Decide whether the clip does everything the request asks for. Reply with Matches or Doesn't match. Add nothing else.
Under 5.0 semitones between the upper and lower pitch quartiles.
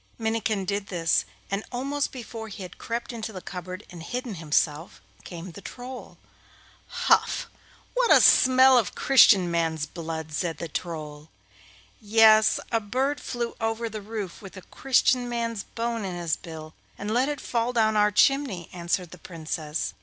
Doesn't match